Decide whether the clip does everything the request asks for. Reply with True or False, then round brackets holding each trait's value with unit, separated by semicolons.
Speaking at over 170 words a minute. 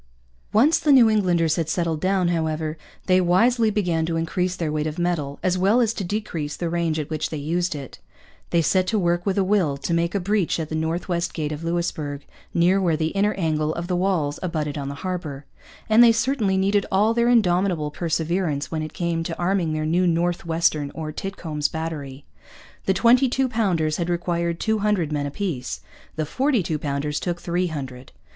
True (205 wpm)